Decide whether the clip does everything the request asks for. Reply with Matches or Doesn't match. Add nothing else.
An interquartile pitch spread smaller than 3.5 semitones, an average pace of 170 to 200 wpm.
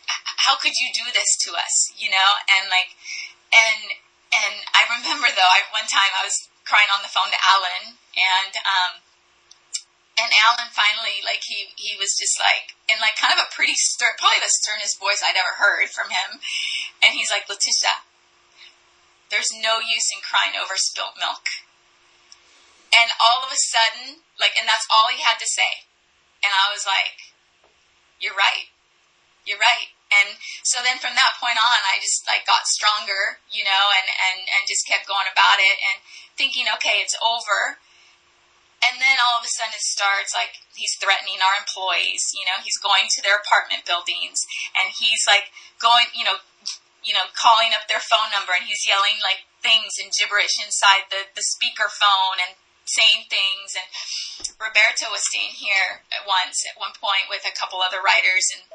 Matches